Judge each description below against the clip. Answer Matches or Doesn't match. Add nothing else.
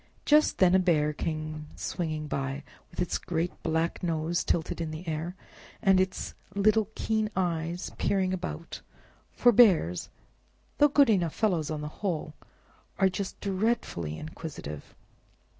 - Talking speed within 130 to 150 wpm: Matches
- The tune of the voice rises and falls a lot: Doesn't match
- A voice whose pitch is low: Doesn't match